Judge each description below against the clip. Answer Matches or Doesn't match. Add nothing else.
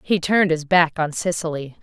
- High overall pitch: Doesn't match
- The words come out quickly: Doesn't match